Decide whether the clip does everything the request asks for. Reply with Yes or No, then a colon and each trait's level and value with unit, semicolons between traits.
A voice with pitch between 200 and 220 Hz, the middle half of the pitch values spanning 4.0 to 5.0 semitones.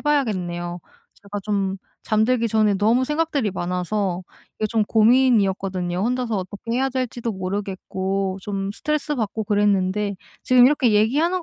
Yes: high, 210 Hz; average, 4.4 semitones